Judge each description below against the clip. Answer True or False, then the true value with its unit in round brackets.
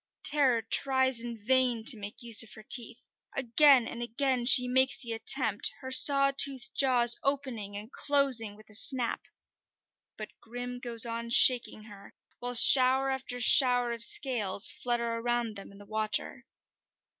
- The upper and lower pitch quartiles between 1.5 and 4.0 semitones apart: True (2.6 semitones)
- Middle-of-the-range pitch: False (240 Hz)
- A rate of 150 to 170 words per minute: True (155 wpm)